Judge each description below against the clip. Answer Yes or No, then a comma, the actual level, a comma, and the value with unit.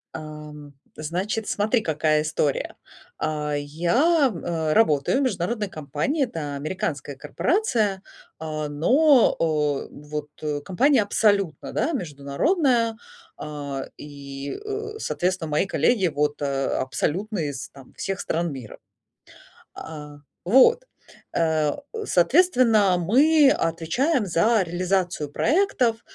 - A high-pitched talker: No, medium, 170 Hz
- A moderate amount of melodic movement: No, wide, 7.7 semitones